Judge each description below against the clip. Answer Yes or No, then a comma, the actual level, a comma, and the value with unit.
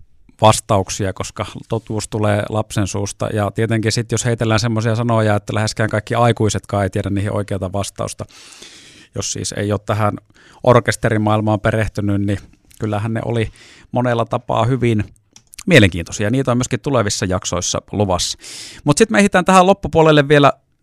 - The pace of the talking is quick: No, average, 145 wpm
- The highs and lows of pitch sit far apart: No, narrow, 2.6 semitones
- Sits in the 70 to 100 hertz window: No, low, 110 Hz